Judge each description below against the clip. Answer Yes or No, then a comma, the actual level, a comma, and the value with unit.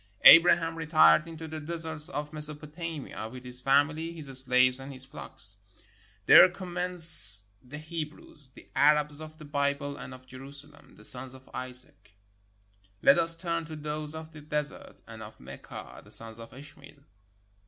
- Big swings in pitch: No, average, 3.5 semitones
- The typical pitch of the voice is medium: Yes, medium, 150 Hz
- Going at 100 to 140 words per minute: No, average, 160 wpm